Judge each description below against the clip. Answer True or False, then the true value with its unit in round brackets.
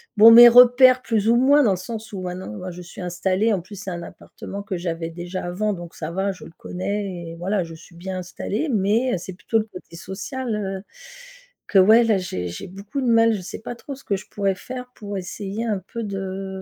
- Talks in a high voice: True (195 Hz)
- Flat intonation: False (3.7 semitones)